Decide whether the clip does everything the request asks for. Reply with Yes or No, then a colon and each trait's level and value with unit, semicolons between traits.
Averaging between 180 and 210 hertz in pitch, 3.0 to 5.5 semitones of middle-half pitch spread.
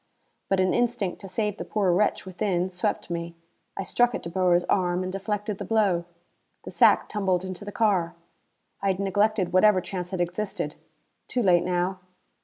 No: high, 190 Hz; narrow, 2.6 semitones